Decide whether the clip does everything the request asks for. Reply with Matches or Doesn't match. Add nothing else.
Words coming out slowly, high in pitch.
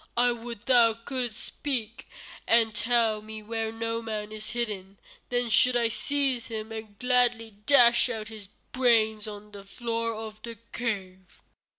Doesn't match